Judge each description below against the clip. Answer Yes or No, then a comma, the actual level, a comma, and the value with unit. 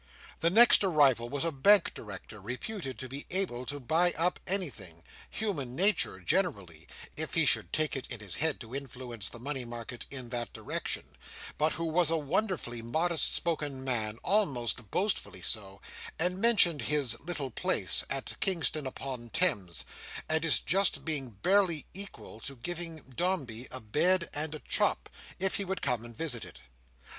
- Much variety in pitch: Yes, wide, 6.6 semitones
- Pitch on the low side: No, medium, 145 Hz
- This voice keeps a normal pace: Yes, average, 160 wpm